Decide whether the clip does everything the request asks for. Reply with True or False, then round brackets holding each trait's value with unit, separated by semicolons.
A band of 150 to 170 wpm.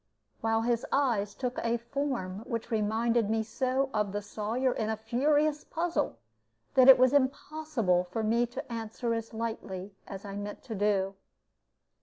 True (160 wpm)